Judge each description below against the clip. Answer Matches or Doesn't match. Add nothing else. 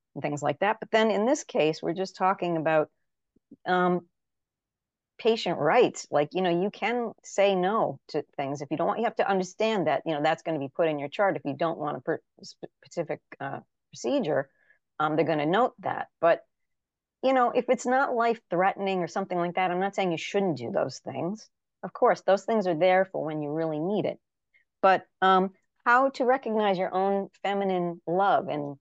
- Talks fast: Matches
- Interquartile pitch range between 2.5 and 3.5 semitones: Doesn't match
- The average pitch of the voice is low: Doesn't match